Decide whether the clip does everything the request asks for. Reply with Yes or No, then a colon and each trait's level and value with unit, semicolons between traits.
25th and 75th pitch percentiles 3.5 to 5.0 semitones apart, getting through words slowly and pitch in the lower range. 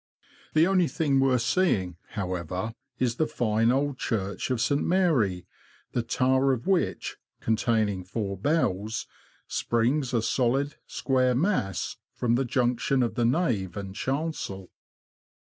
Yes: average, 4.7 semitones; slow, 130 wpm; low, 120 Hz